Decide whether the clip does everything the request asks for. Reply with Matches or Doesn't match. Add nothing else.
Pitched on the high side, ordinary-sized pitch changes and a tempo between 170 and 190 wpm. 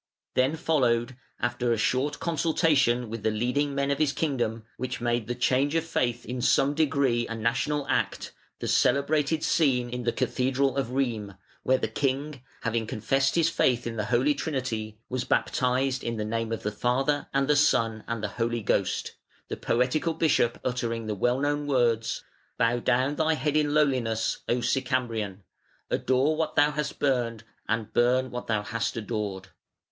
Doesn't match